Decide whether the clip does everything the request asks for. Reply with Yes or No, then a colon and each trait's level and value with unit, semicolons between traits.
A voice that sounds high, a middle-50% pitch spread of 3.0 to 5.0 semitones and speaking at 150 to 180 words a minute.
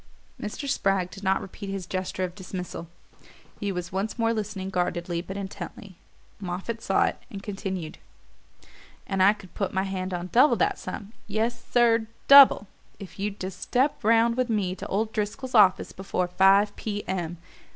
No: high, 195 Hz; narrow, 2.6 semitones; average, 170 wpm